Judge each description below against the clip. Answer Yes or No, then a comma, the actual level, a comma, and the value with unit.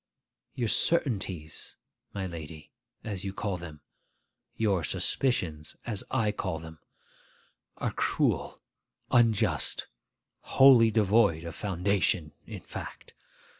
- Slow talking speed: Yes, slow, 100 wpm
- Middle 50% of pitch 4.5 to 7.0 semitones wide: Yes, average, 5.2 semitones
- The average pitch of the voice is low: Yes, very low, 95 Hz